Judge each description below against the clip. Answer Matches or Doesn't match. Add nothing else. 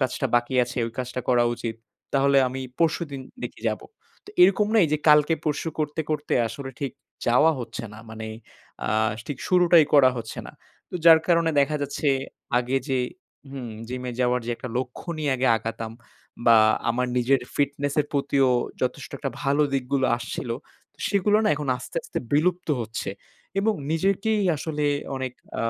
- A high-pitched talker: Doesn't match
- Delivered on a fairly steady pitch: Doesn't match